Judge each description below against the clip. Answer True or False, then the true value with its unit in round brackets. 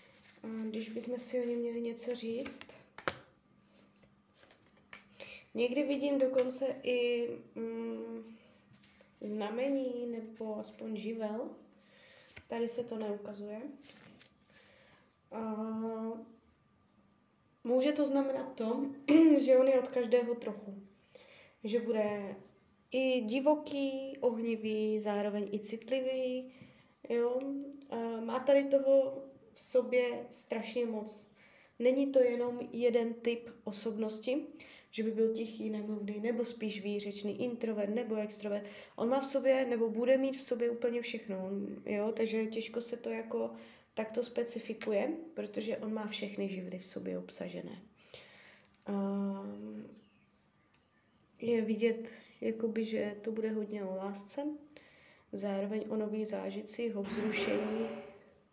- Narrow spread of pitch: False (3.1 semitones)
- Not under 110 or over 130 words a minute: True (115 wpm)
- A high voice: True (230 Hz)